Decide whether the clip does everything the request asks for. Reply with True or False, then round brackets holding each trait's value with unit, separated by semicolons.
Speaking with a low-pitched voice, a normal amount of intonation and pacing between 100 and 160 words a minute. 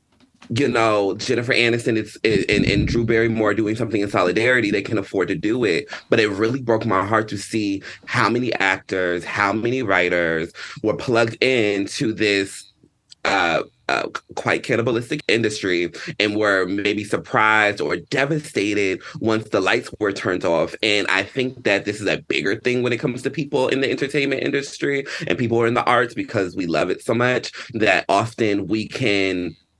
False (110 Hz; 3.3 semitones; 180 wpm)